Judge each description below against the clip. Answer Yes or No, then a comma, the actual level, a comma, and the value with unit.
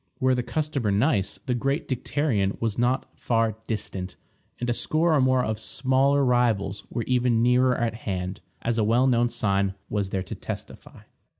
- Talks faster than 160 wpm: Yes, average, 175 wpm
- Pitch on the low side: Yes, low, 120 Hz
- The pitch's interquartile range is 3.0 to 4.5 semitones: Yes, average, 3.7 semitones